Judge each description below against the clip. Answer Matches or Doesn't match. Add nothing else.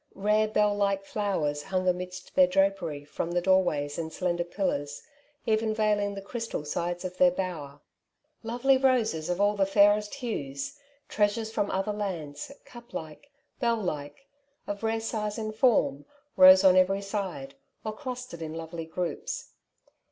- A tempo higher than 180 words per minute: Doesn't match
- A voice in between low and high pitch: Doesn't match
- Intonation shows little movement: Doesn't match